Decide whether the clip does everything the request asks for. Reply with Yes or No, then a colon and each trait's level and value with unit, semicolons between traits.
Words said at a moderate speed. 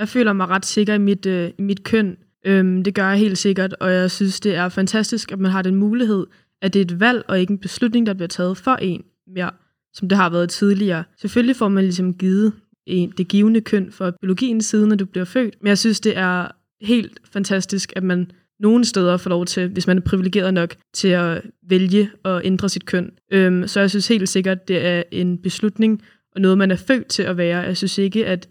No: fast, 230 wpm